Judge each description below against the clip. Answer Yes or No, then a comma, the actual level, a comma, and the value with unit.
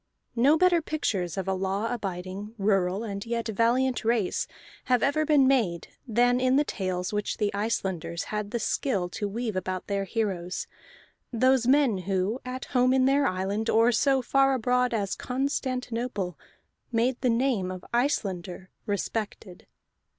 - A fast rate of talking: No, average, 150 wpm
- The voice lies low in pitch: No, high, 225 Hz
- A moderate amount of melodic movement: Yes, average, 4.8 semitones